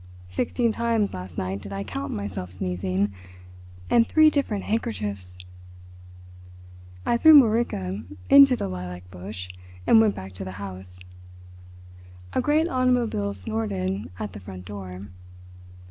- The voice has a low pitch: Yes, low, 100 Hz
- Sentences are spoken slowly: Yes, slow, 130 wpm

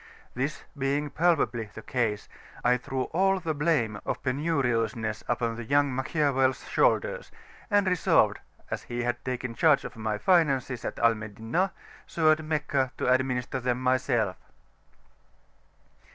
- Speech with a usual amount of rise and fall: Yes, average, 4.5 semitones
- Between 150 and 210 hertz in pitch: No, low, 130 Hz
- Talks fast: No, average, 140 wpm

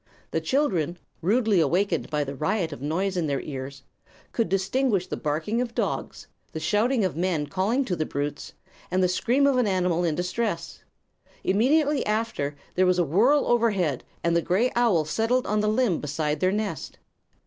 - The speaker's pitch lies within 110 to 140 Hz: No, medium, 185 Hz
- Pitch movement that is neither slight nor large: No, wide, 6.1 semitones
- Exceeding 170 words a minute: Yes, average, 180 wpm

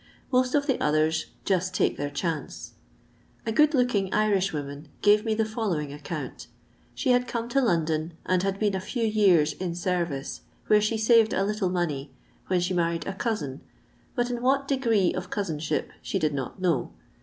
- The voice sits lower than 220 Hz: Yes, high, 190 Hz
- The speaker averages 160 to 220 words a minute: Yes, average, 180 wpm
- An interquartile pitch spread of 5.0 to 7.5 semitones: Yes, wide, 5.6 semitones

